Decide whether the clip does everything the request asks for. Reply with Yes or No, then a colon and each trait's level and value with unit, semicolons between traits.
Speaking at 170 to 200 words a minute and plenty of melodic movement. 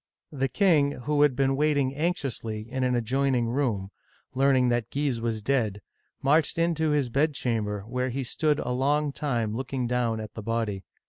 No: average, 175 wpm; average, 3.6 semitones